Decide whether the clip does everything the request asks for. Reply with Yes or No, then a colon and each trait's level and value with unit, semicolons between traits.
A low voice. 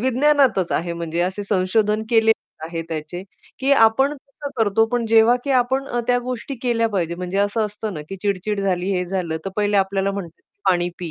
No: high, 205 Hz